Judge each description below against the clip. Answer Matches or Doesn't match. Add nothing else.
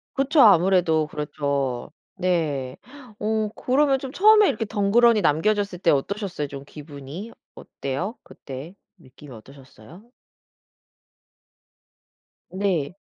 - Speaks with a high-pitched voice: Doesn't match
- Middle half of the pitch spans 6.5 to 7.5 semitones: Matches